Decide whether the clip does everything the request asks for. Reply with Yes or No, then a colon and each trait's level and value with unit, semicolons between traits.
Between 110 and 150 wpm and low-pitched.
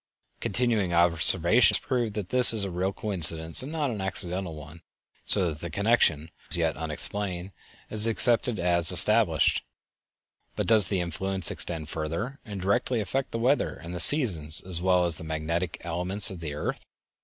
No: average, 175 wpm; very low, 90 Hz